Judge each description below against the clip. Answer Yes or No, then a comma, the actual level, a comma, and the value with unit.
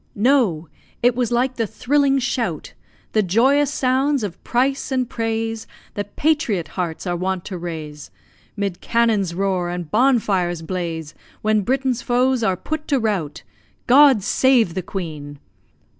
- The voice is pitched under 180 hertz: No, high, 220 Hz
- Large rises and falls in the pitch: Yes, wide, 6.3 semitones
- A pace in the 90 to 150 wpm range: Yes, average, 145 wpm